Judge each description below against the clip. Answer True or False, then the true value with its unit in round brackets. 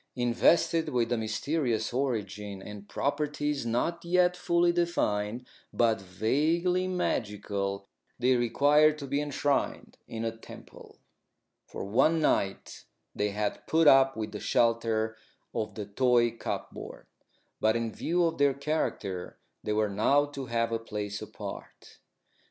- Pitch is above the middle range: False (120 Hz)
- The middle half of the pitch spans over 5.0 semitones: True (5.5 semitones)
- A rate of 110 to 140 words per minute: True (135 wpm)